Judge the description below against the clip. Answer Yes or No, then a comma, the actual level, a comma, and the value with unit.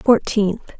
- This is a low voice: No, high, 210 Hz